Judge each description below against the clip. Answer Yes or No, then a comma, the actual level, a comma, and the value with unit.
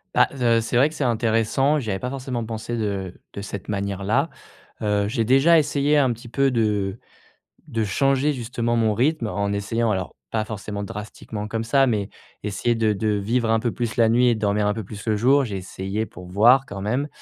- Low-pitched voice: Yes, low, 115 Hz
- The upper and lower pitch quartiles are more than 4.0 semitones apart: No, average, 3.4 semitones